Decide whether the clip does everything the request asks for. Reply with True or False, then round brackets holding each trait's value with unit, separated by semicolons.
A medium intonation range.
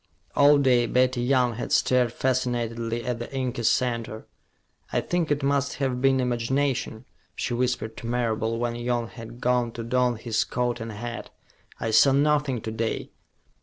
False (2.0 semitones)